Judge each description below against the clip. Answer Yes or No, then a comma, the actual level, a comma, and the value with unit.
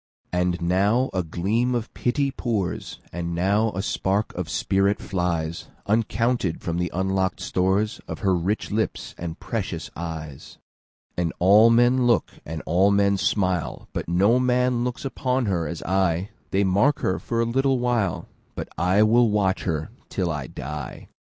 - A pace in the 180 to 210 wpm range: No, average, 140 wpm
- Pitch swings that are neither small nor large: Yes, average, 4.8 semitones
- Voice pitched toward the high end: No, very low, 95 Hz